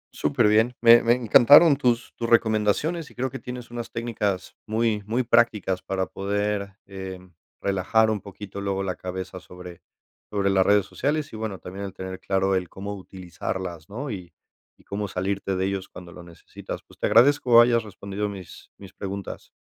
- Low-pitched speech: Yes, low, 100 Hz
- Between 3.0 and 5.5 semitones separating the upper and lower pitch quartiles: Yes, average, 3.6 semitones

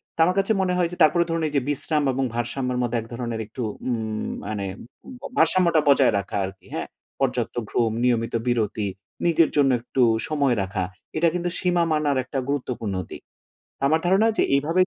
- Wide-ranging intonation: Yes, wide, 5.9 semitones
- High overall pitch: No, low, 135 Hz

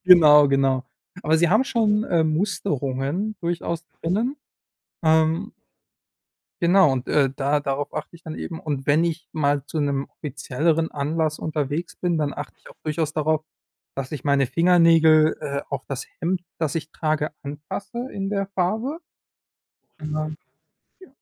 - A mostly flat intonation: No, average, 3.2 semitones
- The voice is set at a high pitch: No, medium, 155 Hz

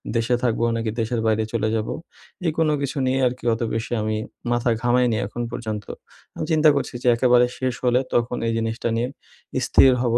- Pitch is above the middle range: No, low, 120 Hz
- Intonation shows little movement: Yes, narrow, 1.9 semitones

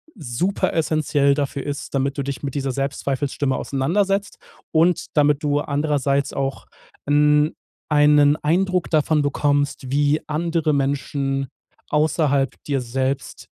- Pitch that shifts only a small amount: Yes, narrow, 1.8 semitones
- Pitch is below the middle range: No, medium, 145 Hz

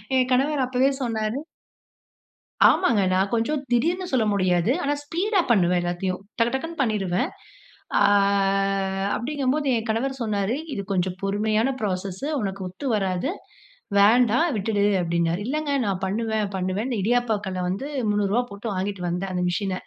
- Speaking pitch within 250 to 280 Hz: No, high, 215 Hz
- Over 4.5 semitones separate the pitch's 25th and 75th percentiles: Yes, average, 5.0 semitones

